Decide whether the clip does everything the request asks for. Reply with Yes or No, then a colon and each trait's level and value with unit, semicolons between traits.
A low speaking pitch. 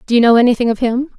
No: high, 240 Hz